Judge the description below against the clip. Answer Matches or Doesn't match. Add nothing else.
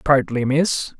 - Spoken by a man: Matches